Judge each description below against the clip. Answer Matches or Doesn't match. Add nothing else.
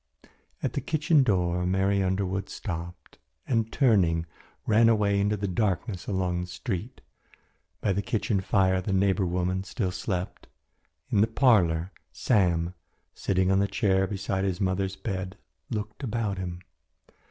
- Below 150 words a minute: Matches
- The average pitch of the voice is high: Doesn't match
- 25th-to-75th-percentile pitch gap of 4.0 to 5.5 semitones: Doesn't match